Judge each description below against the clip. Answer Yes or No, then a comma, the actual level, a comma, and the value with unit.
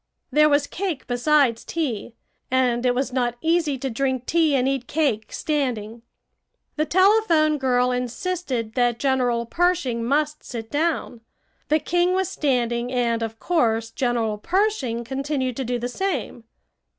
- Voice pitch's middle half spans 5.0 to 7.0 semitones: No, average, 4.4 semitones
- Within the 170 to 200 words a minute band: No, average, 145 wpm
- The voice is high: Yes, very high, 260 Hz